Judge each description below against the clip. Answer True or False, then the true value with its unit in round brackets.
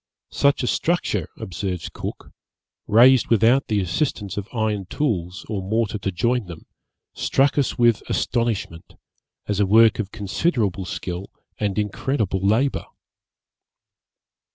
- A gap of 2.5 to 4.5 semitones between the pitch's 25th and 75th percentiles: True (3.7 semitones)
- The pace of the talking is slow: True (125 wpm)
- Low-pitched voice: True (105 Hz)